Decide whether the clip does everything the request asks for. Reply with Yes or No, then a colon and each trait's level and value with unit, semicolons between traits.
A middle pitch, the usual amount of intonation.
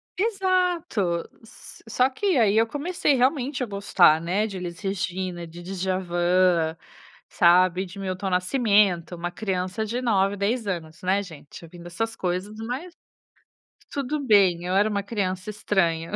No: high, 195 Hz; average, 4.3 semitones